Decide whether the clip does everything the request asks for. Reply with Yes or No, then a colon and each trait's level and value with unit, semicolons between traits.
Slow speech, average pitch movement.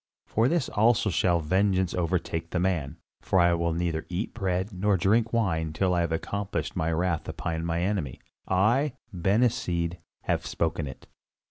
No: average, 165 wpm; average, 3.5 semitones